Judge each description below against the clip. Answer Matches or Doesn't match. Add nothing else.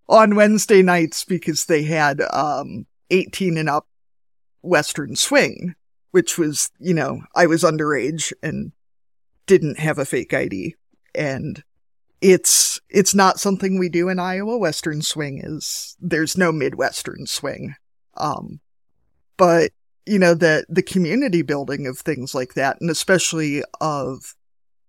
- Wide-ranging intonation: Doesn't match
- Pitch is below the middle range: Doesn't match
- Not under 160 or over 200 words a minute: Doesn't match